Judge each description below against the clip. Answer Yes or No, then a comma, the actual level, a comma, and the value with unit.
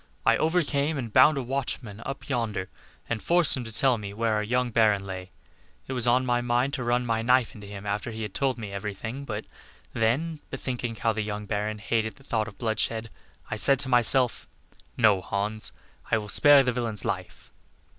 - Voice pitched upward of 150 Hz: No, low, 115 Hz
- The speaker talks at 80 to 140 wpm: No, fast, 205 wpm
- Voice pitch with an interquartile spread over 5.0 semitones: No, average, 3.4 semitones